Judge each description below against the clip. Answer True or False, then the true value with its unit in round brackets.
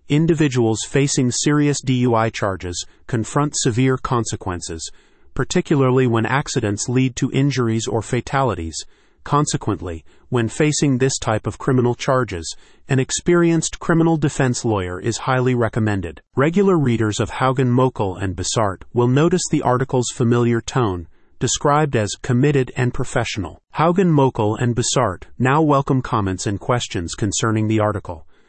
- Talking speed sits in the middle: False (130 wpm)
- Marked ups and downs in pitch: False (4.2 semitones)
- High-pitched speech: False (125 Hz)